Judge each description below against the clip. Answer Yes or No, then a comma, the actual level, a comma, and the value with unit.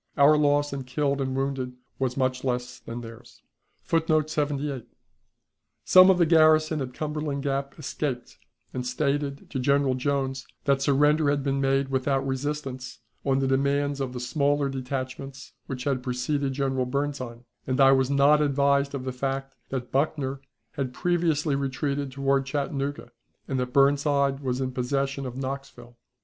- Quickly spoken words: No, average, 160 wpm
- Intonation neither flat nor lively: No, narrow, 1.6 semitones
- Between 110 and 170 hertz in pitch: Yes, low, 135 Hz